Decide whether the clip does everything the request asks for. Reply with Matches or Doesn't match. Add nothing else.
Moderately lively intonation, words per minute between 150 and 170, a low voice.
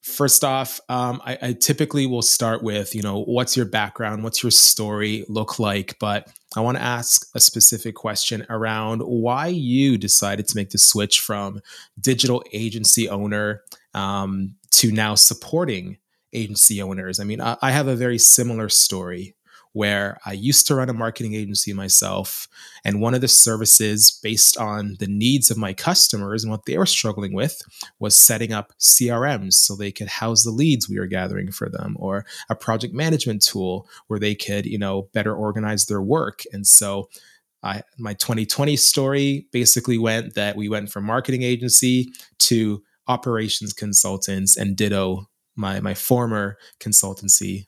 Matches